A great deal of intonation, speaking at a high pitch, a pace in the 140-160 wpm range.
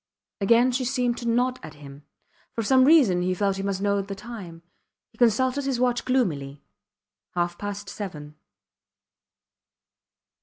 Yes: wide, 5.8 semitones; high, 205 Hz; average, 145 wpm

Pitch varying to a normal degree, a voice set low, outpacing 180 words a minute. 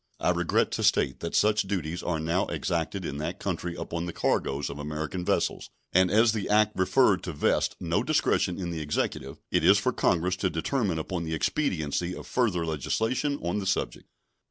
Yes: average, 4.1 semitones; very low, 90 Hz; average, 190 wpm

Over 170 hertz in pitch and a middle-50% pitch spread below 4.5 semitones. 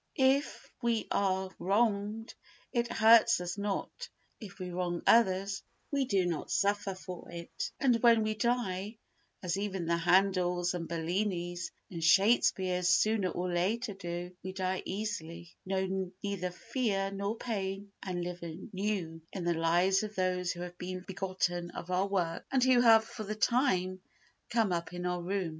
Yes: high, 190 Hz; average, 3.1 semitones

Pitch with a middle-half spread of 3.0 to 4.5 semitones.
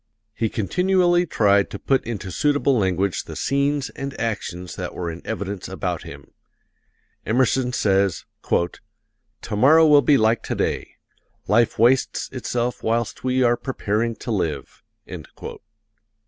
No: average, 5.1 semitones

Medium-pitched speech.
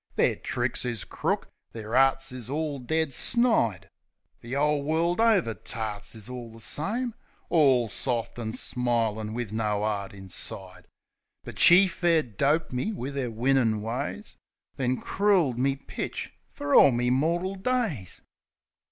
No: low, 130 Hz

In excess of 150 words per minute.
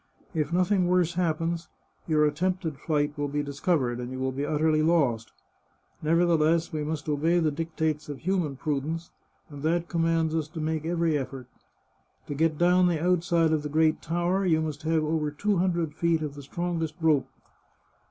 Yes: average, 180 wpm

